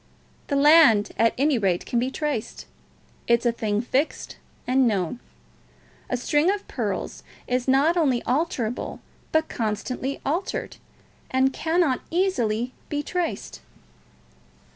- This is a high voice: Yes, very high, 260 Hz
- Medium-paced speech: No, slow, 125 wpm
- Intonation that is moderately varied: Yes, average, 4.7 semitones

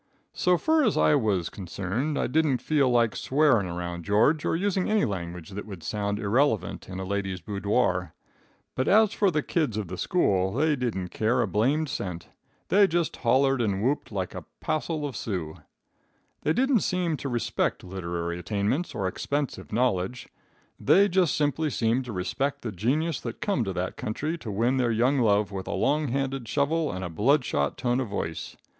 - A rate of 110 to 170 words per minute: No, average, 185 wpm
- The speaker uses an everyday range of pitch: No, wide, 7.4 semitones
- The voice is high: No, low, 120 Hz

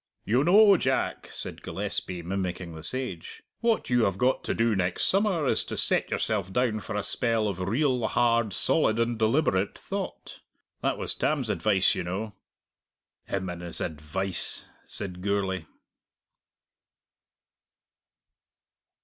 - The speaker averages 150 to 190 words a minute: No, slow, 135 wpm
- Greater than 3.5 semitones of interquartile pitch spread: Yes, average, 5.1 semitones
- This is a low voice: Yes, low, 105 Hz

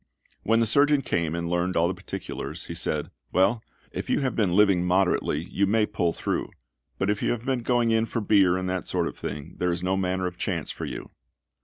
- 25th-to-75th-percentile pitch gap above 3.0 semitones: Yes, average, 4.2 semitones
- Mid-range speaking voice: No, very low, 95 Hz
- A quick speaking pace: Yes, fast, 225 wpm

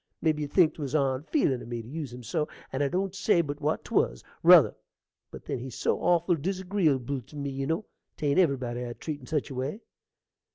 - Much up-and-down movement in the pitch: No, average, 4.1 semitones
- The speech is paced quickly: Yes, fast, 210 wpm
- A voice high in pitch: No, medium, 145 Hz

